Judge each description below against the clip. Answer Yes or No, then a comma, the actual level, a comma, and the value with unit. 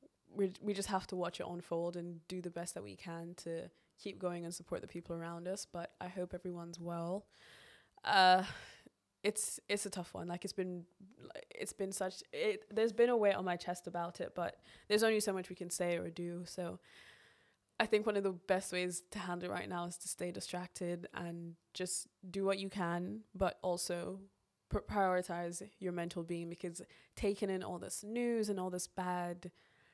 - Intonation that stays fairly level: Yes, narrow, 2.2 semitones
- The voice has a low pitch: No, medium, 180 Hz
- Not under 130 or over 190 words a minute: No, average, 200 wpm